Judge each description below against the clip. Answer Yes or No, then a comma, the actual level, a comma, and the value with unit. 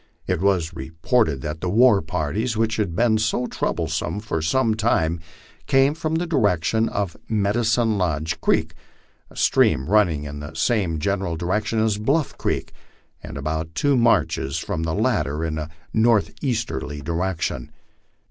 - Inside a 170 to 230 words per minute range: No, average, 155 wpm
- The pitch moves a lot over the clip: Yes, wide, 5.8 semitones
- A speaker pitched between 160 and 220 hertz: No, low, 100 Hz